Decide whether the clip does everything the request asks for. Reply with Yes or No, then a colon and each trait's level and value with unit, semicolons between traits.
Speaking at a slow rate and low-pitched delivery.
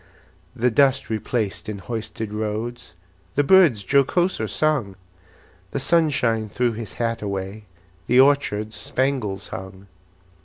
Yes: slow, 115 wpm; low, 115 Hz